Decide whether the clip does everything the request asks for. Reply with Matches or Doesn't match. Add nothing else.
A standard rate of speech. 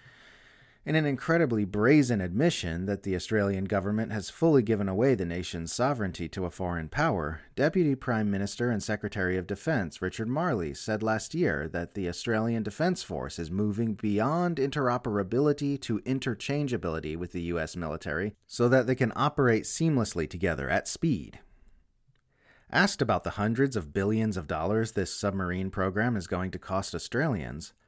Matches